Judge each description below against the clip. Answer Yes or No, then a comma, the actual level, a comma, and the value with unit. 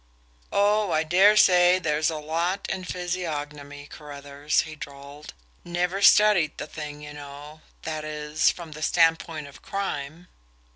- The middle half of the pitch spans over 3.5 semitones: No, average, 3.2 semitones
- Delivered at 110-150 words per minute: Yes, average, 140 wpm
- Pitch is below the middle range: No, medium, 155 Hz